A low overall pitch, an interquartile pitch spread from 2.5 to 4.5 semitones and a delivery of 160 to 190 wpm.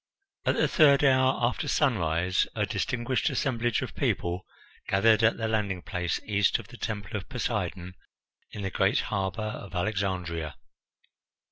No: low, 105 Hz; average, 4.1 semitones; average, 145 wpm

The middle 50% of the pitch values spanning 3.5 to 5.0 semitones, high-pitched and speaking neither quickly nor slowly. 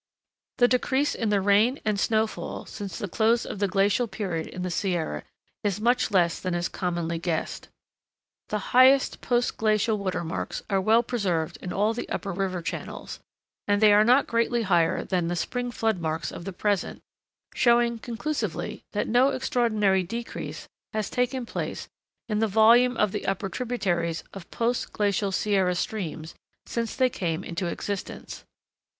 Yes: average, 4.4 semitones; high, 205 Hz; average, 160 wpm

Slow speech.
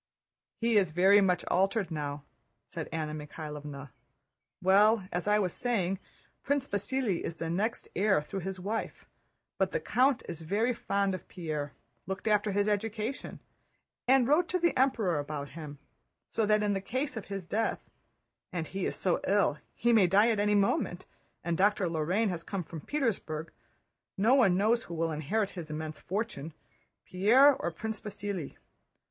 No: average, 165 wpm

